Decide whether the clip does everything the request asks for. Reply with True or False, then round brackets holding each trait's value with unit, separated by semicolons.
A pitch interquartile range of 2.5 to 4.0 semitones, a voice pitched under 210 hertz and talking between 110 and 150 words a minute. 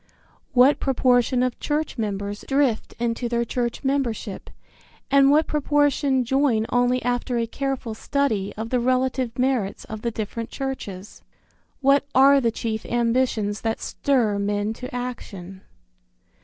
False (3.3 semitones; 245 Hz; 135 wpm)